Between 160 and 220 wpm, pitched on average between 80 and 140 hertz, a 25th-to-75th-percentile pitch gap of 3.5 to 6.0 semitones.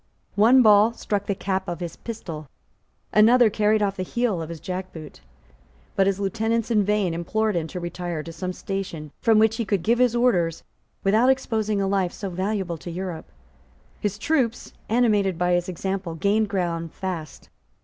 No: average, 175 wpm; high, 195 Hz; average, 3.8 semitones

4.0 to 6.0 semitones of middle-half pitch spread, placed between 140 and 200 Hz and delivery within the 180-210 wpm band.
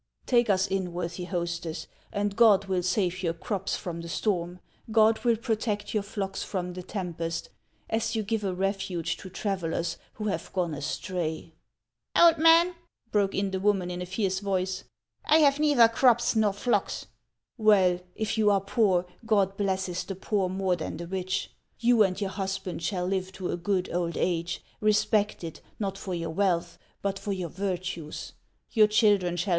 No: average, 2.9 semitones; high, 190 Hz; average, 185 wpm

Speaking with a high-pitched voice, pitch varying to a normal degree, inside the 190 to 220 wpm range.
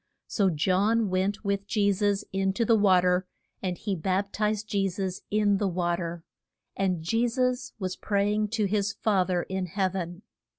No: high, 195 Hz; narrow, 2.3 semitones; average, 195 wpm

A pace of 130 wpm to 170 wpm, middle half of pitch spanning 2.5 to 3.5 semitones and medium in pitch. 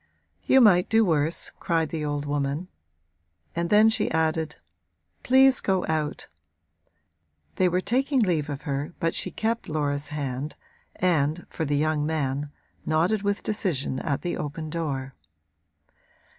No: average, 140 wpm; average, 4.1 semitones; medium, 160 Hz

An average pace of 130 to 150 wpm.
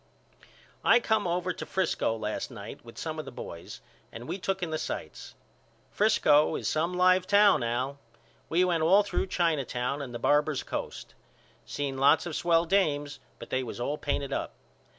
No: average, 180 wpm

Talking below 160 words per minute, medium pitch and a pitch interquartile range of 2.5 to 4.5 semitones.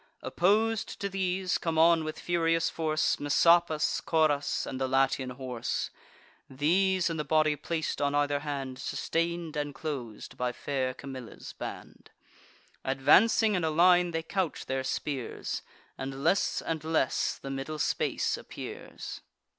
Yes: average, 140 wpm; medium, 155 Hz; average, 4.0 semitones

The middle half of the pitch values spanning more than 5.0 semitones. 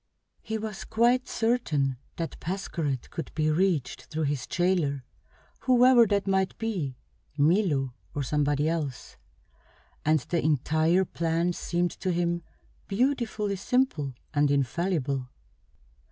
Yes: wide, 5.4 semitones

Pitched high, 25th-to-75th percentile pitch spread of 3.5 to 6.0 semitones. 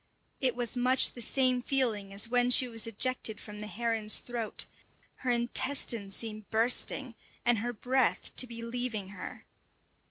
No: high, 235 Hz; narrow, 2.4 semitones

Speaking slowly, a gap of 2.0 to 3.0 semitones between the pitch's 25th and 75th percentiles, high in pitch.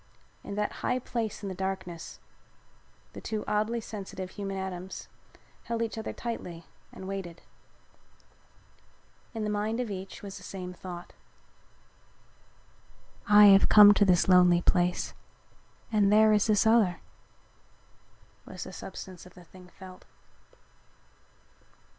Yes: slow, 130 wpm; average, 2.7 semitones; high, 195 Hz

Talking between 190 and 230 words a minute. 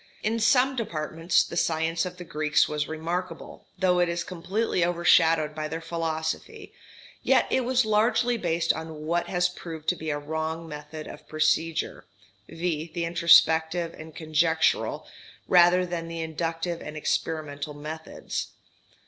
No: average, 145 wpm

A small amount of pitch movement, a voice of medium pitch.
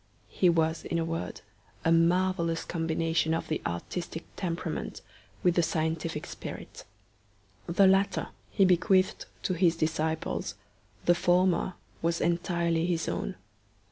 Yes: narrow, 1.6 semitones; medium, 170 Hz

